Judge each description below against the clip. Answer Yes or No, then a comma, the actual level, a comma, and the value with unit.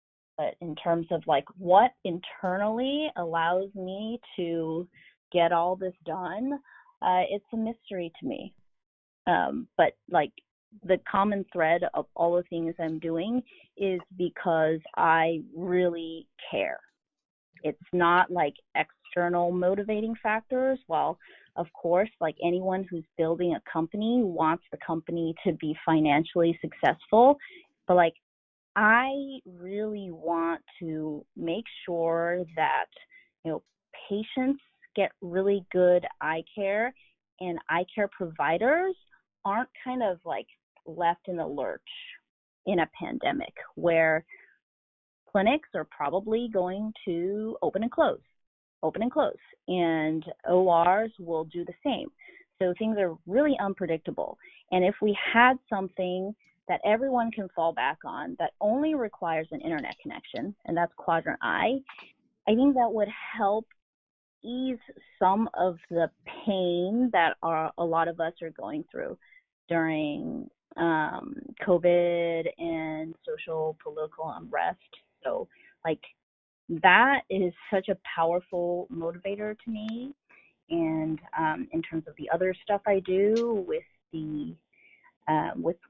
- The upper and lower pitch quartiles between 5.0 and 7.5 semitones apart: Yes, wide, 5.4 semitones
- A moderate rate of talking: No, slow, 130 wpm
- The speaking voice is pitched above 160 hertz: Yes, medium, 185 Hz